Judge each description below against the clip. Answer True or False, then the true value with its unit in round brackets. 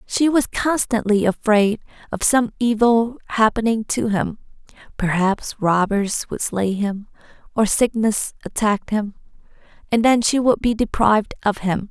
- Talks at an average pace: False (130 wpm)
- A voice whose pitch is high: True (220 Hz)